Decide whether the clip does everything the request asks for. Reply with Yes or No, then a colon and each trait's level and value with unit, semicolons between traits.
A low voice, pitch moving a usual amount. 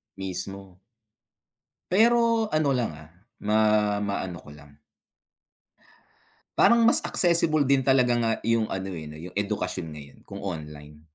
No: low, 100 Hz; wide, 9.0 semitones